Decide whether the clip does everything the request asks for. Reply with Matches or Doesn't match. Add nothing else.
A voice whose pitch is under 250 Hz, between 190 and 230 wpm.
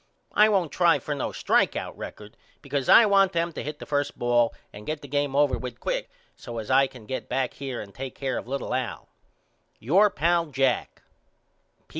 Matches